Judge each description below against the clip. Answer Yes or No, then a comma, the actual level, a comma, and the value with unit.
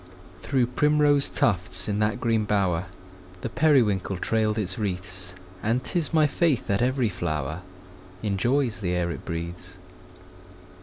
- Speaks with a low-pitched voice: Yes, low, 105 Hz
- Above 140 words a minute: No, slow, 135 wpm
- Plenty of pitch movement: Yes, wide, 5.8 semitones